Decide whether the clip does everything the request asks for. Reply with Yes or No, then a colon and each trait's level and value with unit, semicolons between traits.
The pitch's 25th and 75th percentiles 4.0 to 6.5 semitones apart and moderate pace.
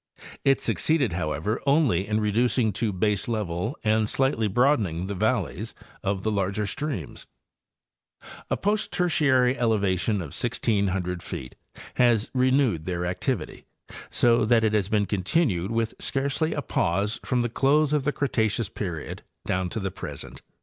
Yes: average, 4.9 semitones; average, 145 wpm